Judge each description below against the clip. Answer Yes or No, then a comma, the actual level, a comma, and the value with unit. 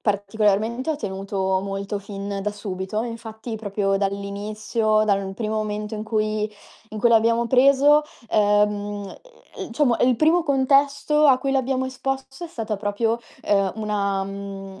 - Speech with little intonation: No, average, 3.9 semitones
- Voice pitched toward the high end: Yes, high, 215 Hz